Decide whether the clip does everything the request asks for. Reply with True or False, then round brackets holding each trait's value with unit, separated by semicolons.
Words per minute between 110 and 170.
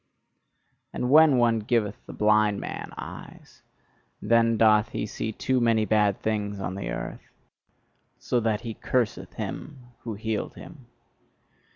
True (140 wpm)